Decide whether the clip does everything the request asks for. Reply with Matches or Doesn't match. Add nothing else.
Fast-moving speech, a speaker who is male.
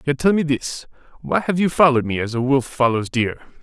Matches